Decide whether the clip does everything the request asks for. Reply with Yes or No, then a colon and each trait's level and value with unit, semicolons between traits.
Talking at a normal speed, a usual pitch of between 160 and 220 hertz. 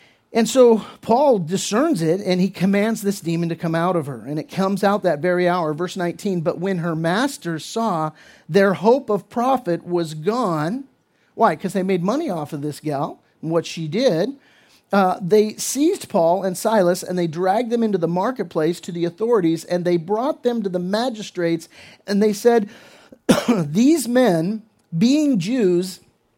Yes: average, 175 wpm; high, 190 Hz